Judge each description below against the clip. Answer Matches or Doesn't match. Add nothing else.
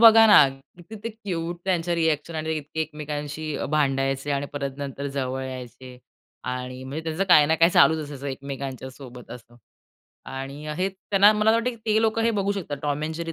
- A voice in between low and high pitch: Matches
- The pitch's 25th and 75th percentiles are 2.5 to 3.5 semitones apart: Doesn't match